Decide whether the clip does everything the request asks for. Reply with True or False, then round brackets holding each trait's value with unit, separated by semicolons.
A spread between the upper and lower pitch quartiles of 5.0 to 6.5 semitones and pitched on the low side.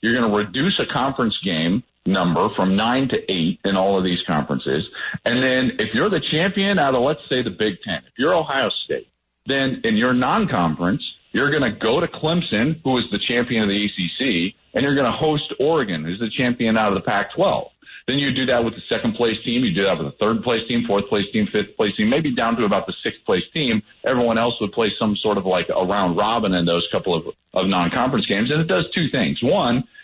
True (5.5 semitones; 120 Hz)